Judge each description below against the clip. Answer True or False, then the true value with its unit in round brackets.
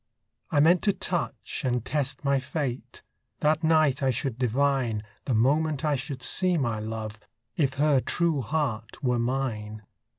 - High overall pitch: False (135 Hz)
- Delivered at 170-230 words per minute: False (155 wpm)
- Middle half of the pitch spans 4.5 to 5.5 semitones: False (4.1 semitones)